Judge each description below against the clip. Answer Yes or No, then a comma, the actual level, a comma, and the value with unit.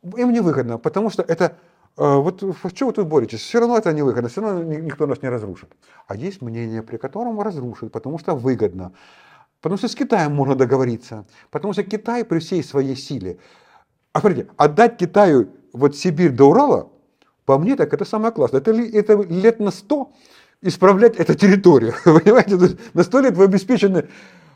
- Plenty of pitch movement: Yes, wide, 7.6 semitones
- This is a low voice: No, medium, 180 Hz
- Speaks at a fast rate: Yes, fast, 185 wpm